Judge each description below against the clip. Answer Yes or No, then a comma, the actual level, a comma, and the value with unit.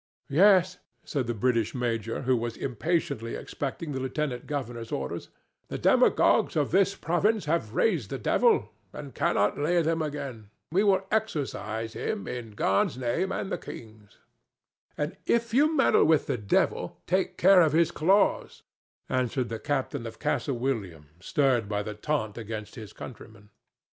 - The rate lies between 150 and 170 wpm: Yes, average, 155 wpm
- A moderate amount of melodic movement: No, wide, 6.8 semitones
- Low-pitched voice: Yes, low, 130 Hz